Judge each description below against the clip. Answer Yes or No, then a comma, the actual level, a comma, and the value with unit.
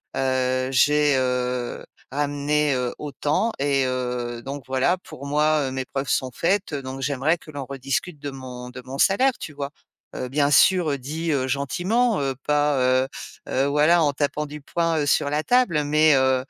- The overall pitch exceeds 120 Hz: Yes, medium, 140 Hz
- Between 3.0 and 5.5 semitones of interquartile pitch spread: No, narrow, 2.6 semitones